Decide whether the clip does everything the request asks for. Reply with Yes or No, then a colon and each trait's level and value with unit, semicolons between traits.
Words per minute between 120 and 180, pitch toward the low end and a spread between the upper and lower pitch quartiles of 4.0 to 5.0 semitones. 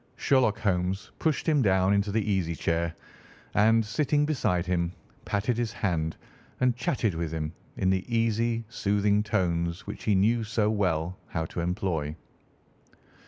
Yes: average, 150 wpm; low, 100 Hz; average, 4.7 semitones